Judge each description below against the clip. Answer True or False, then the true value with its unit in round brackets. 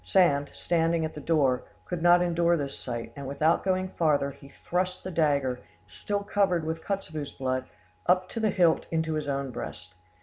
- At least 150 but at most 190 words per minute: True (180 wpm)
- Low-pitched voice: False (160 Hz)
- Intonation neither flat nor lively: True (4.2 semitones)